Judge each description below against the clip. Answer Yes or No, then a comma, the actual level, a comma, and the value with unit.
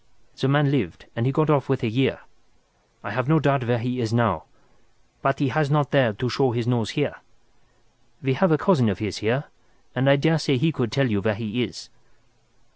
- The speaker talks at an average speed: No, fast, 210 wpm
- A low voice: Yes, low, 130 Hz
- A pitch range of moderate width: Yes, average, 3.4 semitones